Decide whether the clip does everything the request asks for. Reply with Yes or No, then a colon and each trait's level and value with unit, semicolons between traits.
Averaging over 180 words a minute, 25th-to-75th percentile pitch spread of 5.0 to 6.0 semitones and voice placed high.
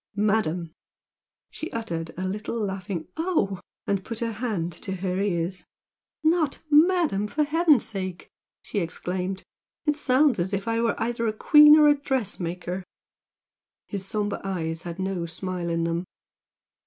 No: average, 150 wpm; average, 5.3 semitones; high, 195 Hz